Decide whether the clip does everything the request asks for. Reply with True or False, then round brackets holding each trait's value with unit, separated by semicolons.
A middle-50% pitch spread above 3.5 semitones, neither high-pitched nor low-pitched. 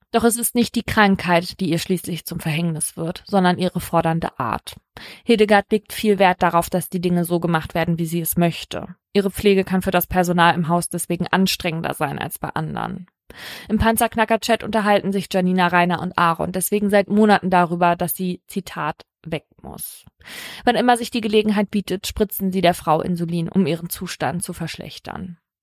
False (3.0 semitones; 180 Hz)